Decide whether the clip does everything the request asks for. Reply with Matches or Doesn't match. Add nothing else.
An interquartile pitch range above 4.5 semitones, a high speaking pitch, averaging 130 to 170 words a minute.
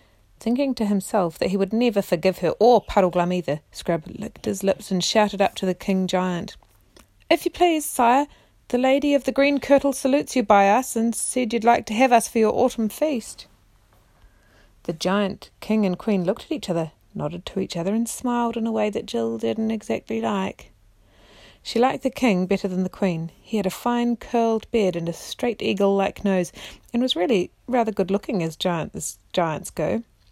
Doesn't match